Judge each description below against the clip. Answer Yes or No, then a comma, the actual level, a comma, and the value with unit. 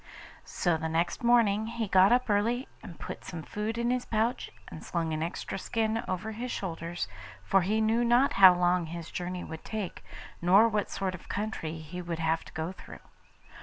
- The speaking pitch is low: No, high, 190 Hz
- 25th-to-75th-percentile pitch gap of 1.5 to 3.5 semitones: No, average, 4.5 semitones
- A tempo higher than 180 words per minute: Yes, average, 195 wpm